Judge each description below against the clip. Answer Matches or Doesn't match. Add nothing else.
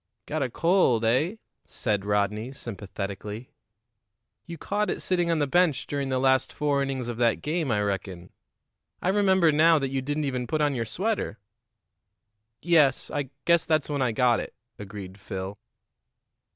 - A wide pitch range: Matches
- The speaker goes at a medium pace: Matches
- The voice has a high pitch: Doesn't match